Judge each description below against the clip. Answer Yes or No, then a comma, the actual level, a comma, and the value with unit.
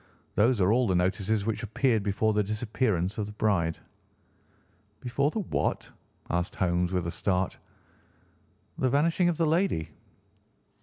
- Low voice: Yes, low, 105 Hz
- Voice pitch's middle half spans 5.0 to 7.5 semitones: Yes, wide, 5.6 semitones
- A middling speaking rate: Yes, average, 145 wpm